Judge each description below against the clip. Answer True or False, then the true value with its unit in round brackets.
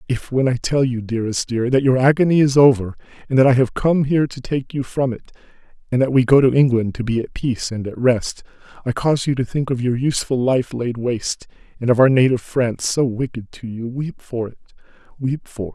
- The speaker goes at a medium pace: False (235 wpm)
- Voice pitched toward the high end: False (125 Hz)